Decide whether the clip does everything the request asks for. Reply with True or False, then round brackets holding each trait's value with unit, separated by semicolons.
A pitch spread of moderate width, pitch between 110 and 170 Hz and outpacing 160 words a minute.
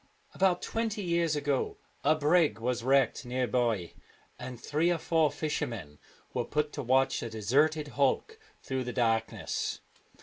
False (4.4 semitones; 140 Hz; 155 wpm)